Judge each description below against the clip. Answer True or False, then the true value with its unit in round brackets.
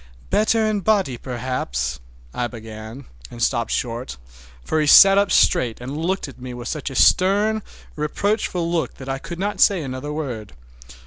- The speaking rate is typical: True (165 wpm)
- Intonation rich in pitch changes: True (7.8 semitones)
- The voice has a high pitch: False (140 Hz)